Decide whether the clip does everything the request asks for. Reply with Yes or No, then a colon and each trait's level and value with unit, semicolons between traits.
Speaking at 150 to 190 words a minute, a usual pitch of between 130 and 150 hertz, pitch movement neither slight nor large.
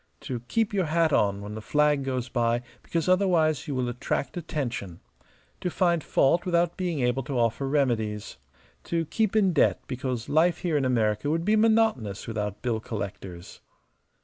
No: average, 170 wpm; low, 135 Hz; wide, 6.6 semitones